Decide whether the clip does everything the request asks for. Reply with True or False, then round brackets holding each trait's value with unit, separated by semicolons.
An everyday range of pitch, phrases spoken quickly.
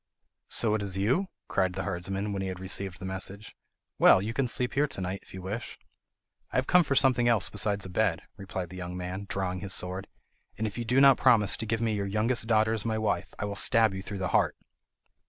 True (3.2 semitones; 240 wpm)